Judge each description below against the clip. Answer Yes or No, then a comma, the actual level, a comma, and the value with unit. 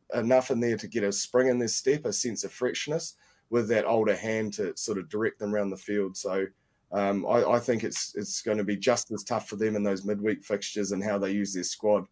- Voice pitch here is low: Yes, low, 105 Hz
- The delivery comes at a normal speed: No, fast, 255 wpm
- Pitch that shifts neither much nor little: Yes, average, 3.0 semitones